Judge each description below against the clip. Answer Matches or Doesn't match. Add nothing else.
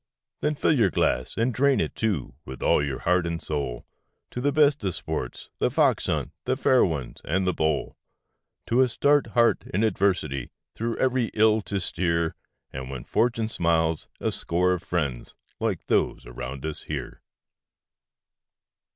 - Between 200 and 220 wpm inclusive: Doesn't match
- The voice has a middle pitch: Doesn't match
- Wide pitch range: Matches